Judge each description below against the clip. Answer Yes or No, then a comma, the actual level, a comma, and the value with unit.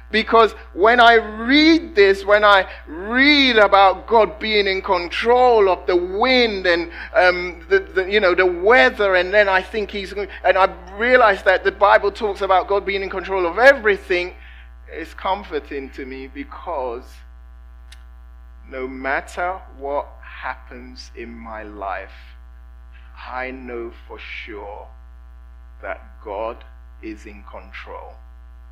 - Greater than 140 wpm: No, slow, 135 wpm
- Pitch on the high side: No, medium, 180 Hz